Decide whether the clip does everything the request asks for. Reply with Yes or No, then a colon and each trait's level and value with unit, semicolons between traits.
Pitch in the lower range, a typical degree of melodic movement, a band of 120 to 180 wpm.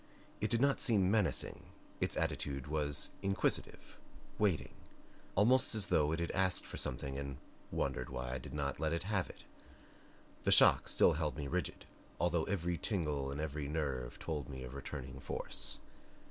Yes: very low, 75 Hz; average, 5.0 semitones; average, 165 wpm